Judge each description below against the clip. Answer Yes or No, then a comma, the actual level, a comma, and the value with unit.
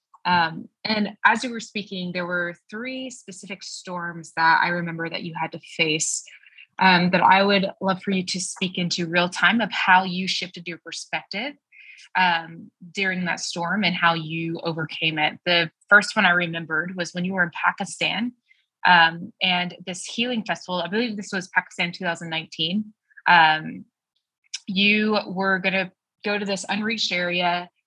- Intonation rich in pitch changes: No, average, 2.8 semitones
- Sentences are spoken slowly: No, average, 170 wpm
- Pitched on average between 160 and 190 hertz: Yes, medium, 185 Hz